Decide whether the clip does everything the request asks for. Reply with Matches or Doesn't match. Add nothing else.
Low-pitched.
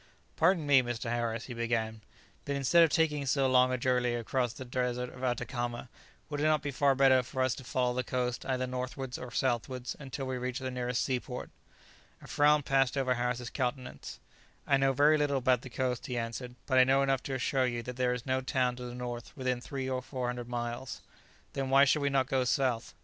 Matches